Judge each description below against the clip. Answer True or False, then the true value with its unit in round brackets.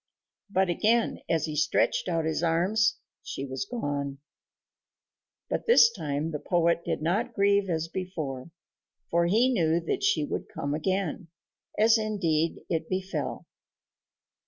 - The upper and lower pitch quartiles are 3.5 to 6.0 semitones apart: True (4.2 semitones)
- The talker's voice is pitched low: False (170 Hz)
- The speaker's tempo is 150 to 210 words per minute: False (135 wpm)